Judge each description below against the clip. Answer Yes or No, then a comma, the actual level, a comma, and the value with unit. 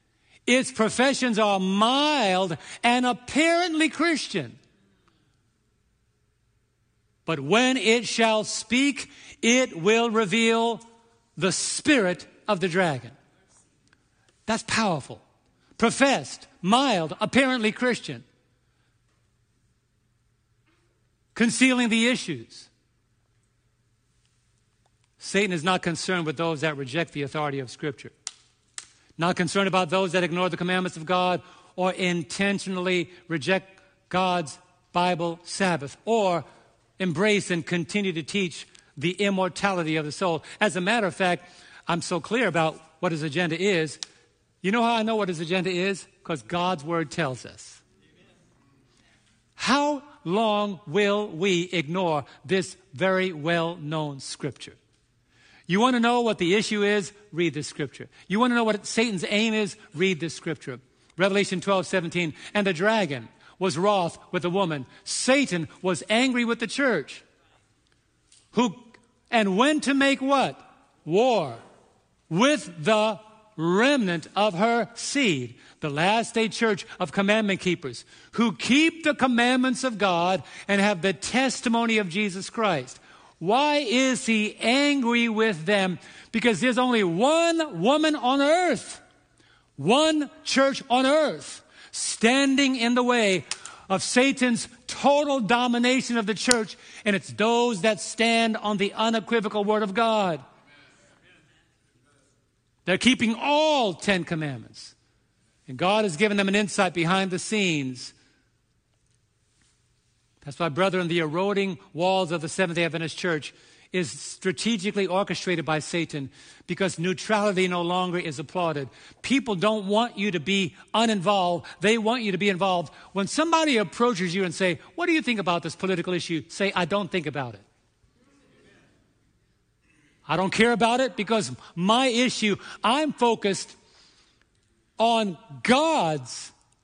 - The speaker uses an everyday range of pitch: No, wide, 5.7 semitones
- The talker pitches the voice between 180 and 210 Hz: Yes, high, 190 Hz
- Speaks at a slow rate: Yes, slow, 130 wpm